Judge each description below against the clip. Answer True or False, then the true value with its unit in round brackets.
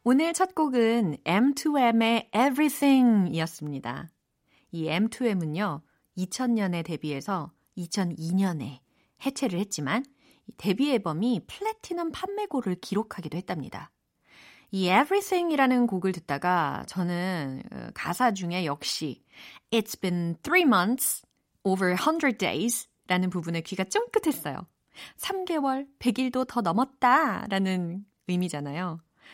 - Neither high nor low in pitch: False (205 Hz)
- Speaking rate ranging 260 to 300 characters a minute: False (310 characters per minute)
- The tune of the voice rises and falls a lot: True (7.2 semitones)